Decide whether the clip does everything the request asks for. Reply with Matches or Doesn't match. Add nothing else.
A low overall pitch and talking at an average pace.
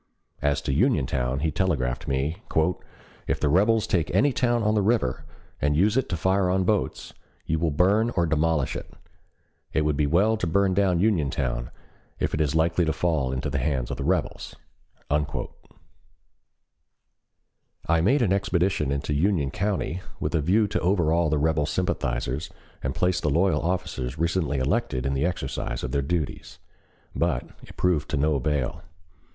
Matches